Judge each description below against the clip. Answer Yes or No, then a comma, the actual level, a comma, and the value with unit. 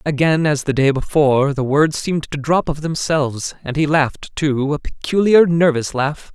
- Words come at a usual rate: Yes, average, 190 wpm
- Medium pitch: Yes, medium, 150 Hz